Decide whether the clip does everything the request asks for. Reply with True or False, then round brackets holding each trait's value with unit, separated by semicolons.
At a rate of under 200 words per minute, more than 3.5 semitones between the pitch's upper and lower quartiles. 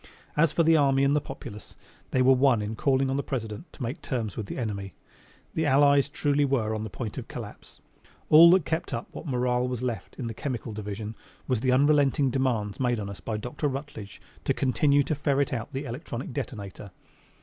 False (205 wpm; 4.2 semitones)